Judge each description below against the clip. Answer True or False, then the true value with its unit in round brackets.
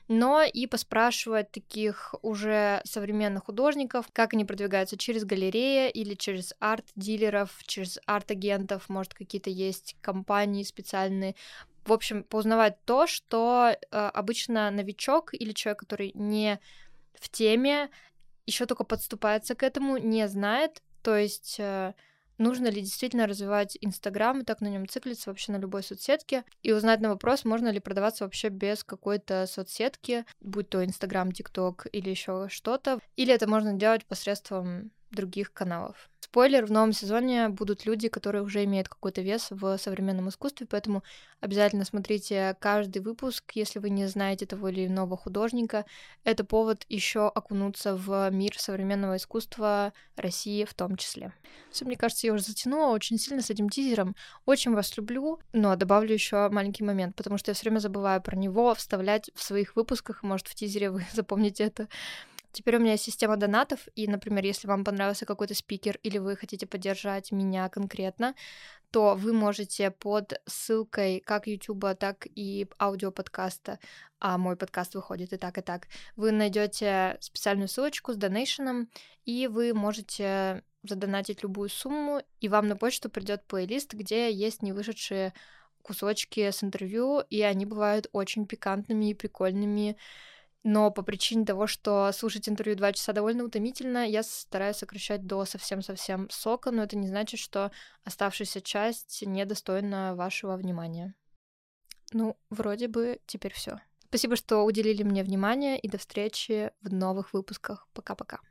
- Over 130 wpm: True (150 wpm)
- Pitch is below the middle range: False (210 Hz)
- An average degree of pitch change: False (2.2 semitones)